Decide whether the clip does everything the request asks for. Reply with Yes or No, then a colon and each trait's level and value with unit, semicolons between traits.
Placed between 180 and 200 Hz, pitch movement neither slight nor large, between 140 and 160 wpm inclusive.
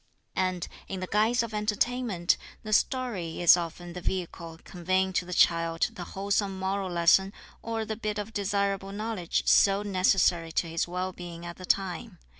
No: high, 190 Hz; average, 3.0 semitones; average, 170 wpm